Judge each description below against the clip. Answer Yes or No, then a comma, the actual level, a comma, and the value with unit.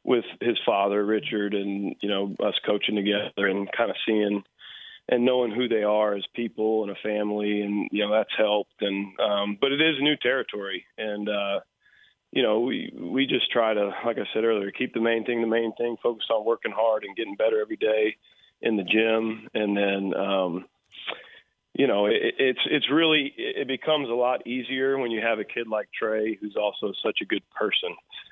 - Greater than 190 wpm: Yes, average, 200 wpm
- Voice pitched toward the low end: Yes, low, 110 Hz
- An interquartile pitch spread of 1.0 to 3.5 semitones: Yes, average, 3.2 semitones